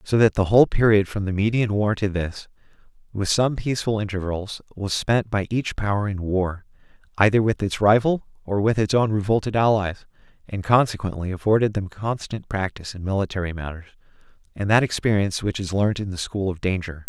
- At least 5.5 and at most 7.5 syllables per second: Yes, 5.6 syllables/s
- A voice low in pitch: Yes, low, 100 Hz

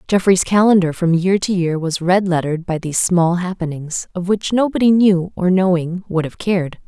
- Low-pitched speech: No, medium, 180 Hz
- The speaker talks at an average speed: Yes, average, 190 wpm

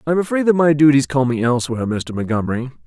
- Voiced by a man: Yes, male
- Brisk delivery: Yes, fast, 230 wpm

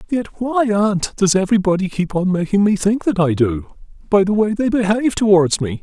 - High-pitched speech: Yes, high, 195 Hz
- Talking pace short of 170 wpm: No, fast, 205 wpm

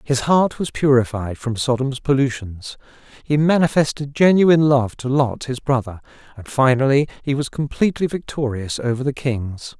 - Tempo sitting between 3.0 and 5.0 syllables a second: Yes, 4.9 syllables/s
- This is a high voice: No, low, 135 Hz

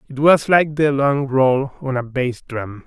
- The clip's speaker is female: No, male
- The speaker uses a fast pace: Yes, fast, 210 wpm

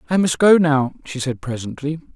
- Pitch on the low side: No, medium, 150 Hz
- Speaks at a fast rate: No, average, 195 wpm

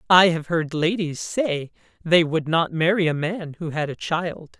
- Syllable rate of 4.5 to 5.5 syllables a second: No, 4.1 syllables/s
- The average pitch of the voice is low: No, medium, 165 Hz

